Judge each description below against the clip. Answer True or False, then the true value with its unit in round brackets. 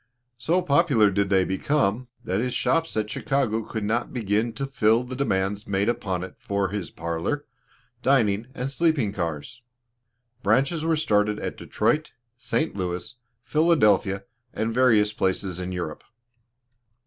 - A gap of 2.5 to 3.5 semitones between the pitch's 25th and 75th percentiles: False (5.6 semitones)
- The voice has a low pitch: True (110 Hz)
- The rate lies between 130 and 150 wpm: True (140 wpm)